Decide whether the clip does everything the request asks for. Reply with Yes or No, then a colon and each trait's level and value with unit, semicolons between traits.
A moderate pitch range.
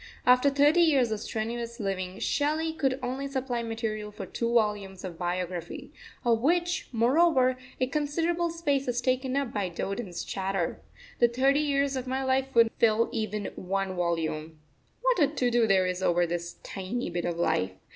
No: wide, 6.1 semitones